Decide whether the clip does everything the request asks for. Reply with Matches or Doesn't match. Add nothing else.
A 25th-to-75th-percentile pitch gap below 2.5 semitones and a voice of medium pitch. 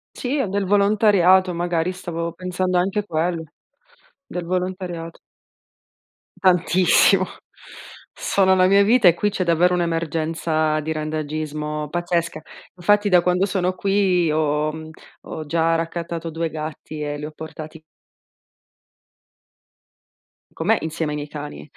Doesn't match